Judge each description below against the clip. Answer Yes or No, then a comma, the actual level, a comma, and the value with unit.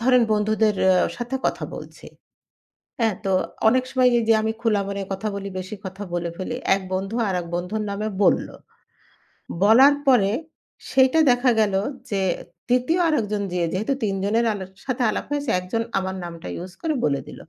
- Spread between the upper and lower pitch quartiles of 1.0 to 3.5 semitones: No, average, 4.2 semitones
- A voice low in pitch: No, high, 215 Hz